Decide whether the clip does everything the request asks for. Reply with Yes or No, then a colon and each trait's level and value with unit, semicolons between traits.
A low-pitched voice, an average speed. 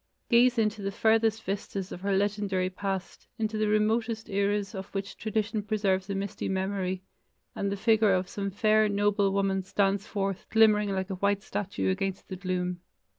No: high, 200 Hz; average, 175 wpm